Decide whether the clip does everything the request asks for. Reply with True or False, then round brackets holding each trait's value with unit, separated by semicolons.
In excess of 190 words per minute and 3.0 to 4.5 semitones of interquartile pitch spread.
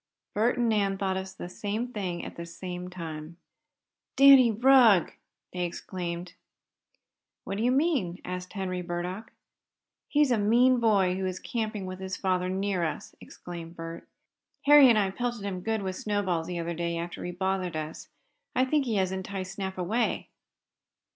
False (165 wpm; 3.8 semitones)